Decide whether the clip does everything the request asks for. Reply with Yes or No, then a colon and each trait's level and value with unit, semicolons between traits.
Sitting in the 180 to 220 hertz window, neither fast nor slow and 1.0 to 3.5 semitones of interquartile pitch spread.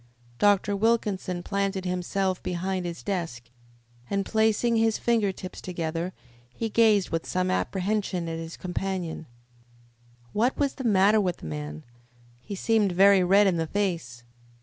Yes: high, 190 Hz; average, 145 wpm; average, 3.0 semitones